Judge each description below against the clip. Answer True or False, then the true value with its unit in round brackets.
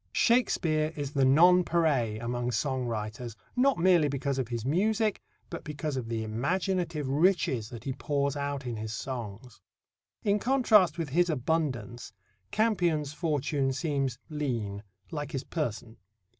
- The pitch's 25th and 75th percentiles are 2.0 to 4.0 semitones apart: False (5.6 semitones)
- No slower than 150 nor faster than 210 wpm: False (140 wpm)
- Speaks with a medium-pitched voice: True (145 Hz)